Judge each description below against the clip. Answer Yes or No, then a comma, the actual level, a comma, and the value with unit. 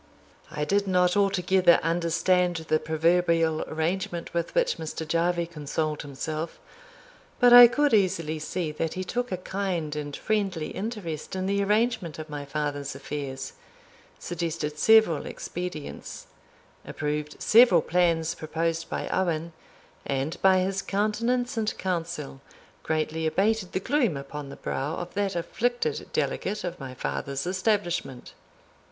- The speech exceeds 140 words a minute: No, slow, 135 wpm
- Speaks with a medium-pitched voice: Yes, medium, 170 Hz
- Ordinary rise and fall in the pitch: Yes, average, 4.0 semitones